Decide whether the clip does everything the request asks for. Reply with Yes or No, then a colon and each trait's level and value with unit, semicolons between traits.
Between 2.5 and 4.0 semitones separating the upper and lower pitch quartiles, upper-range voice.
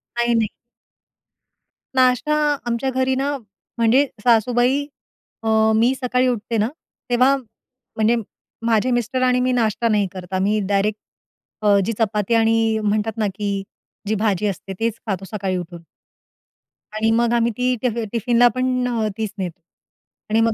Yes: average, 2.9 semitones; high, 225 Hz